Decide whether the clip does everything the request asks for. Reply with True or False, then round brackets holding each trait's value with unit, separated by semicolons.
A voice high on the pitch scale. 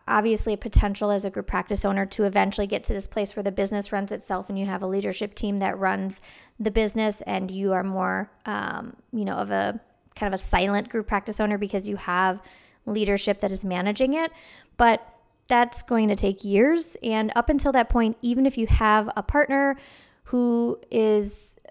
True (210 Hz)